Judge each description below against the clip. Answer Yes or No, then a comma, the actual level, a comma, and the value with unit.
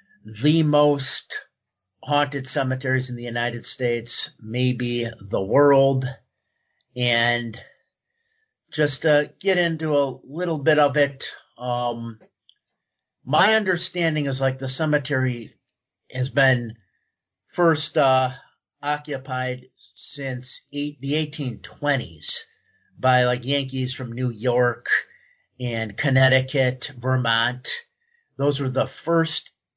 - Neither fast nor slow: No, slow, 100 wpm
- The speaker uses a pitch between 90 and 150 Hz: Yes, low, 135 Hz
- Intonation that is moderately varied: Yes, average, 3.2 semitones